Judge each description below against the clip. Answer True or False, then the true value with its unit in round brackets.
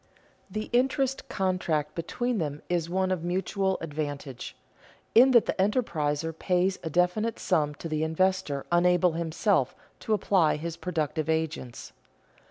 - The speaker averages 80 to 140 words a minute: True (135 wpm)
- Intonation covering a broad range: False (3.6 semitones)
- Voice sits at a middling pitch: True (175 Hz)